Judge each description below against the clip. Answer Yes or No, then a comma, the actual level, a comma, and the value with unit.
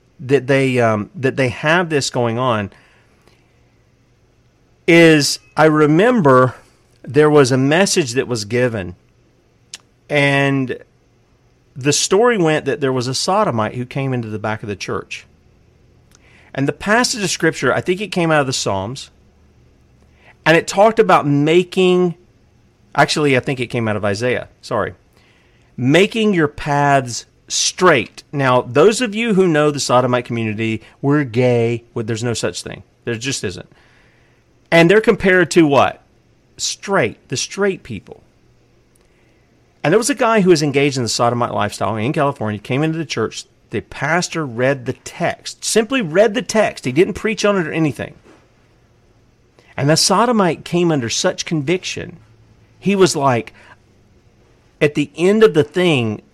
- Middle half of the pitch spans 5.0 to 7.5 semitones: Yes, wide, 5.5 semitones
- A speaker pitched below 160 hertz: Yes, low, 135 Hz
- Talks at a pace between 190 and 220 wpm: No, average, 155 wpm